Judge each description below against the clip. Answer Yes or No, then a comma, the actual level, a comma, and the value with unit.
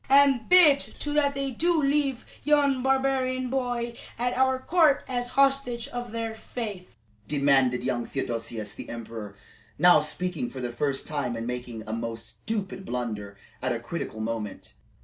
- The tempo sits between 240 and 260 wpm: No, average, 155 wpm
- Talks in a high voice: Yes, high, 220 Hz